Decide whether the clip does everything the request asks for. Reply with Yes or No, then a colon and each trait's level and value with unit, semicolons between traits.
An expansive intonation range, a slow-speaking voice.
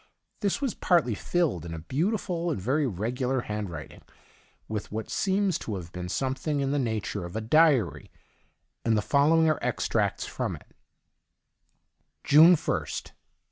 No: wide, 7.5 semitones; average, 150 wpm